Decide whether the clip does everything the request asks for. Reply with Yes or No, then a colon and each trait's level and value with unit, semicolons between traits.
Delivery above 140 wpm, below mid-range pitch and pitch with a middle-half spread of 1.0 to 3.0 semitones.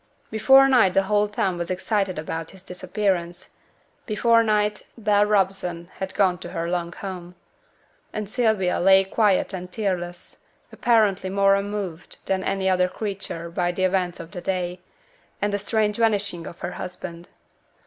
No: average, 160 wpm; high, 190 Hz; narrow, 2.6 semitones